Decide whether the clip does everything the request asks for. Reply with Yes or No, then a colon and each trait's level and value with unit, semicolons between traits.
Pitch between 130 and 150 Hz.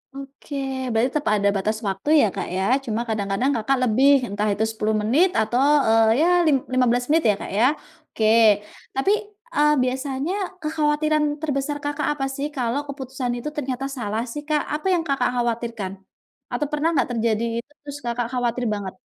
No: very high, 250 Hz